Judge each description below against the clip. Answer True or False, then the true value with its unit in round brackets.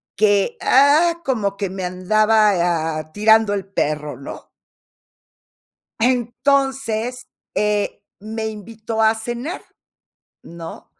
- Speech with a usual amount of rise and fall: True (3.6 semitones)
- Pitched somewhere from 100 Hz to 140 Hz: False (215 Hz)